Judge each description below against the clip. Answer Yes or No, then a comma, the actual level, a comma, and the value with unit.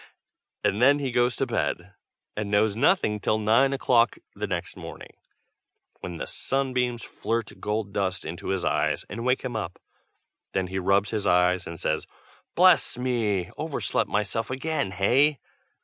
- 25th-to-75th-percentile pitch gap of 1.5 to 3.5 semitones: No, average, 4.6 semitones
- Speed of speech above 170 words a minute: No, average, 155 wpm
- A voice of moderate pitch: No, low, 110 Hz